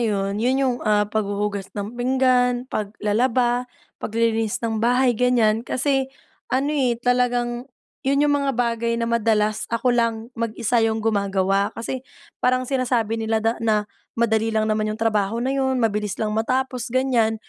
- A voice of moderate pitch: No, high, 230 Hz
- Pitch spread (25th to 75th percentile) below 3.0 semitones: Yes, narrow, 2.6 semitones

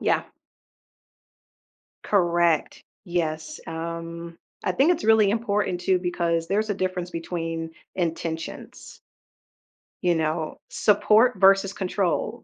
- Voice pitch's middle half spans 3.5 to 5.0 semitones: No, average, 2.9 semitones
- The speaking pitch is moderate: Yes, medium, 175 Hz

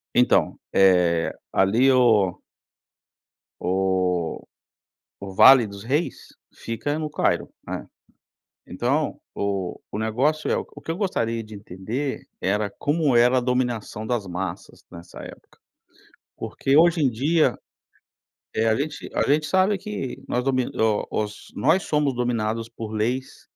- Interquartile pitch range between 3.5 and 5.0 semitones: No, wide, 5.6 semitones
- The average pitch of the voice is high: No, low, 115 Hz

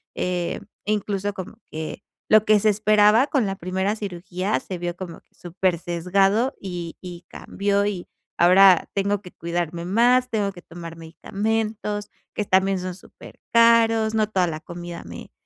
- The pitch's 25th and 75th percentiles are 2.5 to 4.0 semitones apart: Yes, average, 3.2 semitones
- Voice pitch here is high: Yes, high, 195 Hz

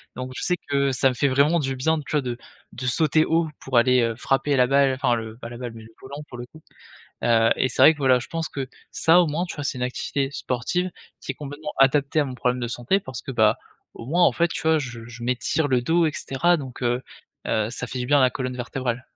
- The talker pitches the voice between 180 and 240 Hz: No, low, 130 Hz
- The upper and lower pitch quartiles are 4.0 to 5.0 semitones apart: No, average, 3.3 semitones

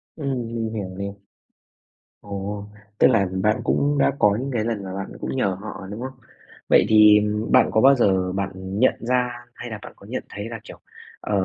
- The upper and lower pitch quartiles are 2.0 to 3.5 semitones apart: Yes, average, 3.0 semitones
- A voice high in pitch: No, low, 105 Hz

